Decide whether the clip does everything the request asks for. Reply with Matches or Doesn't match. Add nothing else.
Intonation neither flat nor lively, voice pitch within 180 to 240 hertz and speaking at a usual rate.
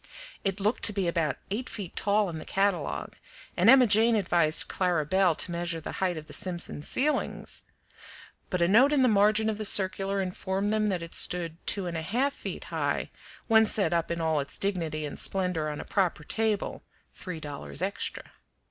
Matches